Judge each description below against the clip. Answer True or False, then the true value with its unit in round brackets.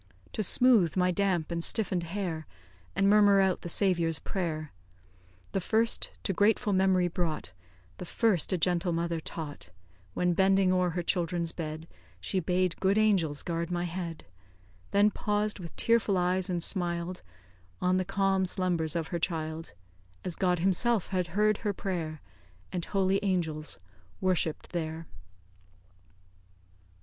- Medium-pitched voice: True (180 Hz)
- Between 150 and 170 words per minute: False (140 wpm)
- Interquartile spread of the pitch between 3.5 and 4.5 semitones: False (2.5 semitones)